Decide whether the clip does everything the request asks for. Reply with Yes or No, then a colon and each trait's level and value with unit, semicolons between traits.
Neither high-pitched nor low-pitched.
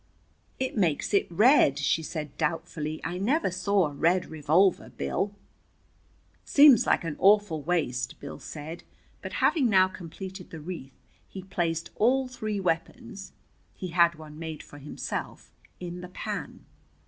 Yes: medium, 175 Hz